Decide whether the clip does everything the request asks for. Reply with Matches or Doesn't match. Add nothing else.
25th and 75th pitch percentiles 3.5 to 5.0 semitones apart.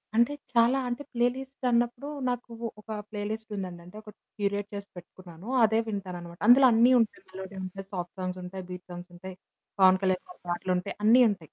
Matches